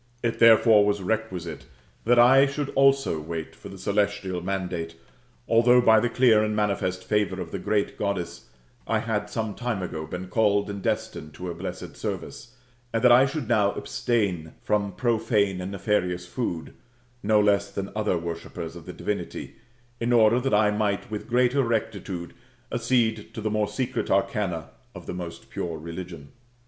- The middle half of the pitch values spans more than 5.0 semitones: No, average, 4.0 semitones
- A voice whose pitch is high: No, low, 105 Hz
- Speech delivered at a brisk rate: No, average, 165 wpm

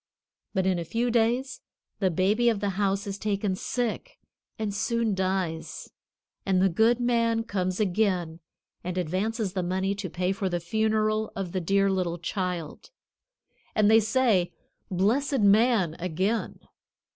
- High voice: Yes, high, 195 Hz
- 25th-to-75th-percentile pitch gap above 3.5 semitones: No, average, 3.2 semitones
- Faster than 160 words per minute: No, average, 145 wpm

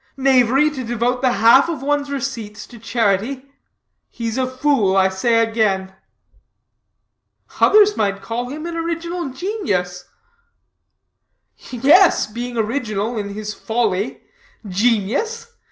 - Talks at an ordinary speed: No, slow, 115 wpm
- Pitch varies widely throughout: No, average, 4.9 semitones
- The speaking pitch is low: No, high, 240 Hz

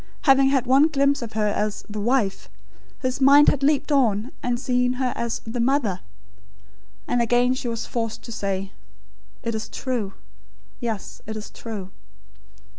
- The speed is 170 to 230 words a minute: No, average, 160 wpm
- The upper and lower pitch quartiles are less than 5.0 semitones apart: Yes, average, 3.5 semitones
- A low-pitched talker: No, high, 240 Hz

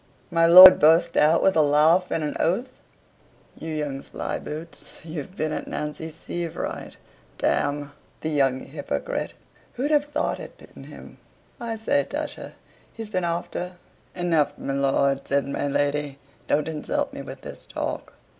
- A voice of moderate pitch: Yes, medium, 160 Hz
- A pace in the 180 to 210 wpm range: No, average, 155 wpm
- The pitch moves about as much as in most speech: Yes, average, 3.4 semitones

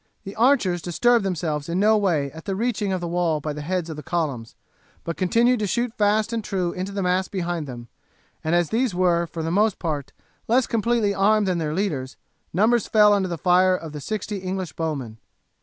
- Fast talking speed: Yes, fast, 210 wpm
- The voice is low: No, medium, 185 Hz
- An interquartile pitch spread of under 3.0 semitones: No, average, 4.4 semitones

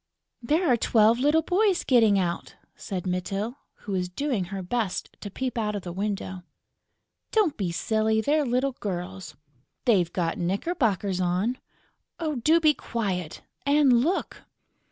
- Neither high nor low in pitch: No, high, 215 Hz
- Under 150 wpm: Yes, average, 140 wpm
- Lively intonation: Yes, wide, 6.2 semitones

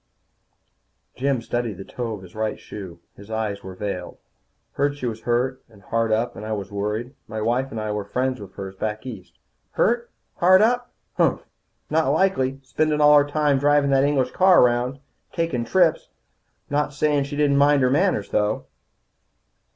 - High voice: No, low, 125 Hz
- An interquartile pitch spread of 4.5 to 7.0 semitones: Yes, average, 5.1 semitones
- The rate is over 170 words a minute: Yes, average, 180 wpm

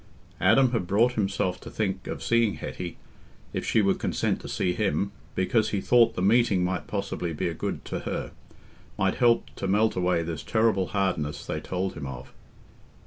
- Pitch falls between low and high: No, very low, 95 Hz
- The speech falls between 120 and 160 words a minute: No, average, 180 wpm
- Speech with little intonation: No, average, 3.5 semitones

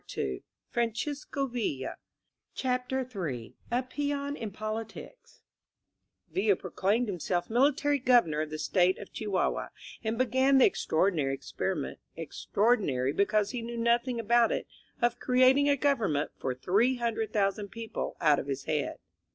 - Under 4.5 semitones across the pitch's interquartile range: No, wide, 5.5 semitones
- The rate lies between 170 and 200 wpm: No, average, 140 wpm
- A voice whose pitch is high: Yes, high, 225 Hz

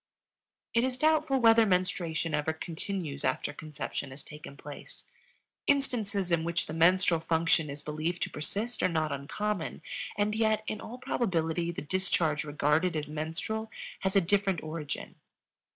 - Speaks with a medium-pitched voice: Yes, medium, 170 Hz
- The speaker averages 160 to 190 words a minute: No, average, 150 wpm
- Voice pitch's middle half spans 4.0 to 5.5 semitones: Yes, average, 5.2 semitones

